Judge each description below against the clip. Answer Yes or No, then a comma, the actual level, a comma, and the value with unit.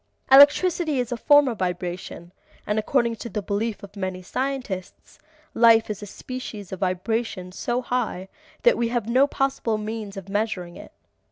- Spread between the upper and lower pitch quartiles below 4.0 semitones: No, average, 4.6 semitones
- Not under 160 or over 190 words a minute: Yes, average, 165 wpm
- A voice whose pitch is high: Yes, high, 220 Hz